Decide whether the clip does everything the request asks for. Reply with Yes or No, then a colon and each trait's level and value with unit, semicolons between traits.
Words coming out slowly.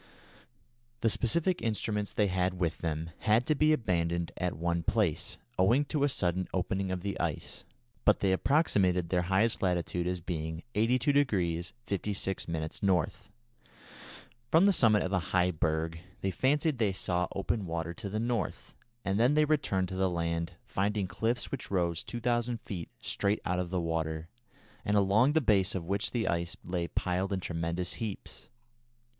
No: average, 165 wpm